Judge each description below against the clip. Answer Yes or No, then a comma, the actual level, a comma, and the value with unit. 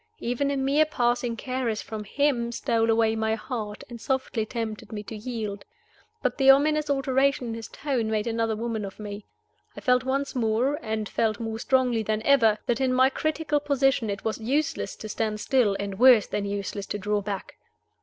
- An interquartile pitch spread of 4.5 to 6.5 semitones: No, average, 3.6 semitones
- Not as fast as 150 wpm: No, average, 190 wpm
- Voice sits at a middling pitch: No, high, 230 Hz